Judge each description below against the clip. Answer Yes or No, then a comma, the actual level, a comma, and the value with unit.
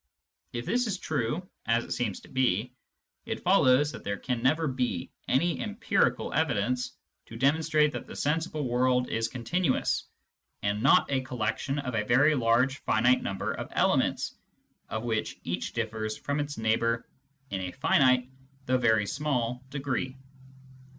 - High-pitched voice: No, low, 125 Hz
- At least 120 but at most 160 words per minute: Yes, average, 150 wpm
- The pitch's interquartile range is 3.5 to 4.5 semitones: Yes, average, 3.8 semitones